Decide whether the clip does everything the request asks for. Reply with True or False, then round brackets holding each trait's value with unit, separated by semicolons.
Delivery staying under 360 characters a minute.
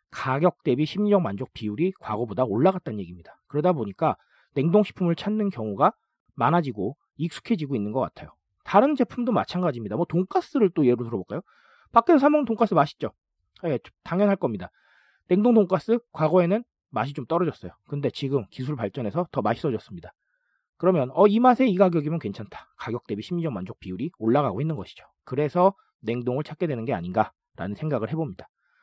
False (405 characters per minute)